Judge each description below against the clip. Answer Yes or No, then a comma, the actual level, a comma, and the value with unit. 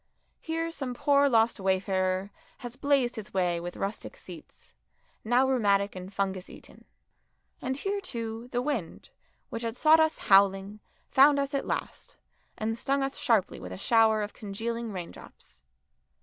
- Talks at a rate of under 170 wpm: Yes, average, 150 wpm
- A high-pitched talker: Yes, high, 225 Hz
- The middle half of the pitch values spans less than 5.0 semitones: No, wide, 5.6 semitones